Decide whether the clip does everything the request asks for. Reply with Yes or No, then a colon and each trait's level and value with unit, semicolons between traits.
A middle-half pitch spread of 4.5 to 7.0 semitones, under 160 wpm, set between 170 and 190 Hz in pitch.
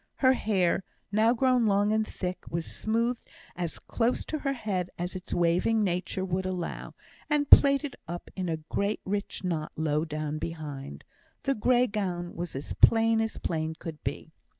No: average, 5.1 semitones; average, 170 wpm; medium, 185 Hz